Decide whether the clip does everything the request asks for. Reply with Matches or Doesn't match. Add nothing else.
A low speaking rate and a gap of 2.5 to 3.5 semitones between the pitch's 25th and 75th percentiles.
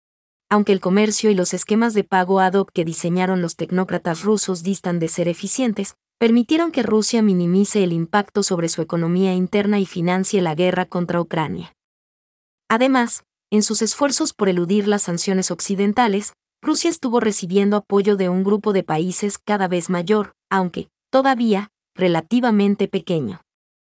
Matches